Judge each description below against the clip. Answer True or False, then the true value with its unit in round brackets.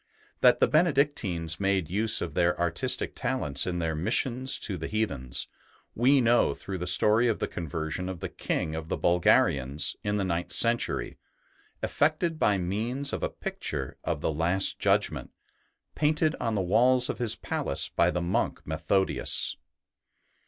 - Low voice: True (95 Hz)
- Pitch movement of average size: False (6.0 semitones)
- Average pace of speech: True (160 wpm)